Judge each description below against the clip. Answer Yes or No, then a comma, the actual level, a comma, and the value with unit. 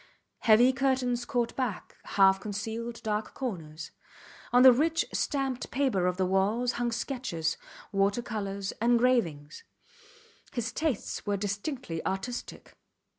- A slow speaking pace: Yes, slow, 120 wpm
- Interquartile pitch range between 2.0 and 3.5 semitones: No, average, 4.4 semitones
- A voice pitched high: Yes, high, 230 Hz